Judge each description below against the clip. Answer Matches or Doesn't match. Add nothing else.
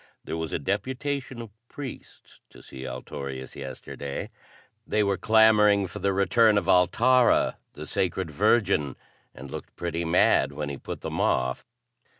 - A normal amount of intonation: Doesn't match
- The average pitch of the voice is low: Matches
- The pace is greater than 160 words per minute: Doesn't match